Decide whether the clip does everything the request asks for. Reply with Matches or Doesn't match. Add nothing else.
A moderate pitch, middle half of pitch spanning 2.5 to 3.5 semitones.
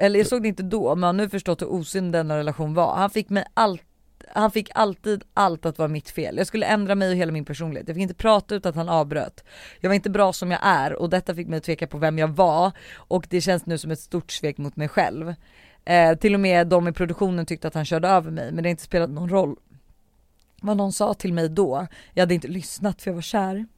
Matches